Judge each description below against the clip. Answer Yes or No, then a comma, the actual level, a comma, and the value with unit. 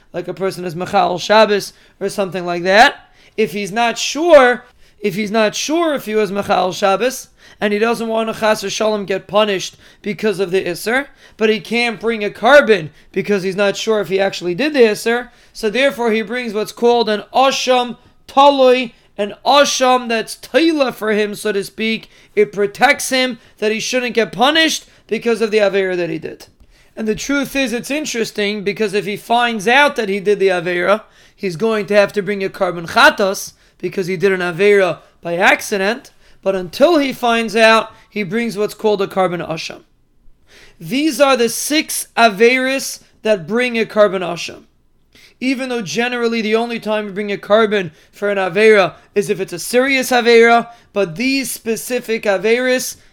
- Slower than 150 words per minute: No, average, 185 wpm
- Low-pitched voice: No, high, 215 Hz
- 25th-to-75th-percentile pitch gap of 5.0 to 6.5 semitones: No, average, 3.3 semitones